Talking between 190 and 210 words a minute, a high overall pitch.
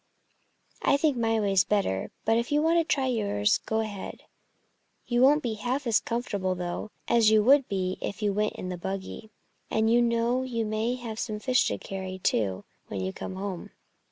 Yes: average, 195 wpm; high, 220 Hz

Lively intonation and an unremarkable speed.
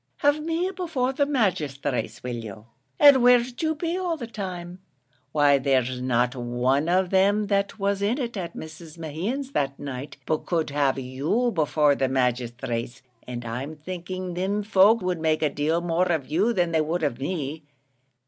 Yes: wide, 7.3 semitones; average, 175 wpm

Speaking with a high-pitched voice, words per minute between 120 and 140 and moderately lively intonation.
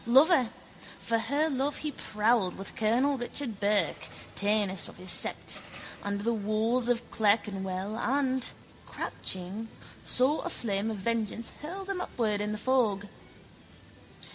Yes: high, 225 Hz; slow, 135 wpm; average, 4.2 semitones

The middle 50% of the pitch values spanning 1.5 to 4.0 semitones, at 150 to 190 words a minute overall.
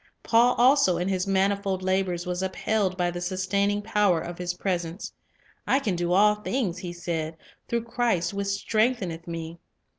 Yes: average, 2.9 semitones; average, 160 wpm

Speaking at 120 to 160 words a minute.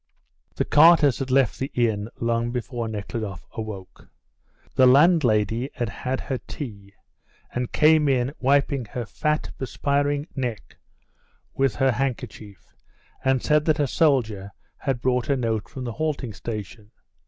Yes: average, 140 wpm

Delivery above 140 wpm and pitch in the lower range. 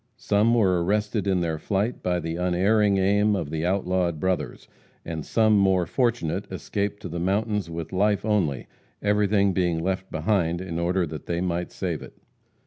Yes: average, 170 wpm; very low, 95 Hz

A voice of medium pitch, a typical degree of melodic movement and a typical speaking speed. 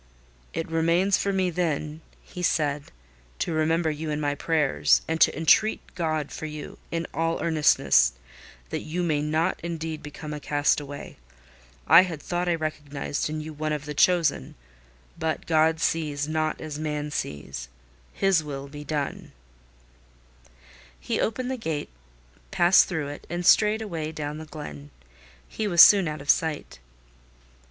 No: medium, 155 Hz; narrow, 2.2 semitones; average, 155 wpm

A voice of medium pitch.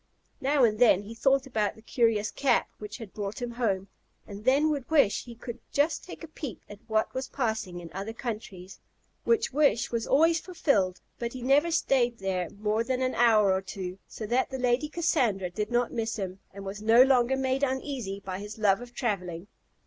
No: high, 230 Hz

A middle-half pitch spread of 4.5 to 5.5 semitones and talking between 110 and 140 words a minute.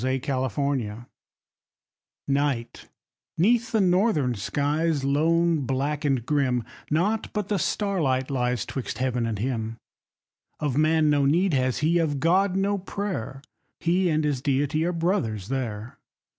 Yes: average, 4.8 semitones; slow, 135 wpm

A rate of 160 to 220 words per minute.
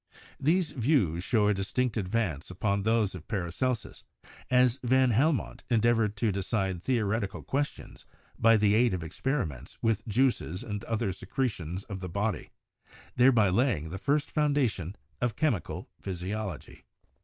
No: average, 145 wpm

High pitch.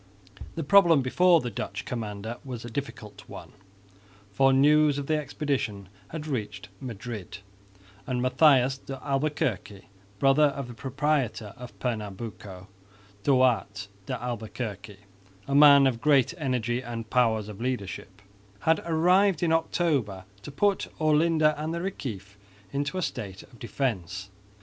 No: low, 130 Hz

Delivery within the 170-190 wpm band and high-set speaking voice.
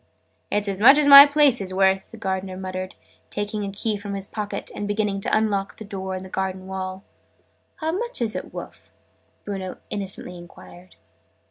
Yes: average, 185 wpm; high, 195 Hz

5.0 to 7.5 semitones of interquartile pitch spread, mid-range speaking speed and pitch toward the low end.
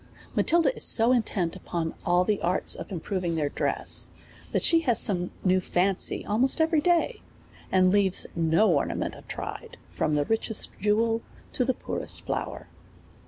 No: average, 5.3 semitones; average, 155 wpm; high, 200 Hz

